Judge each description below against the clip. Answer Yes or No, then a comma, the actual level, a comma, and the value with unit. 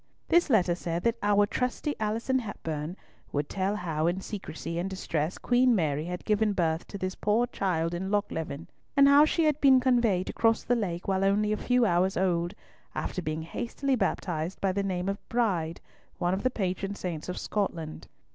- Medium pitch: No, high, 195 Hz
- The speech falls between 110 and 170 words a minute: No, average, 185 wpm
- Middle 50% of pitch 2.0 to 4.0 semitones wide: No, average, 4.7 semitones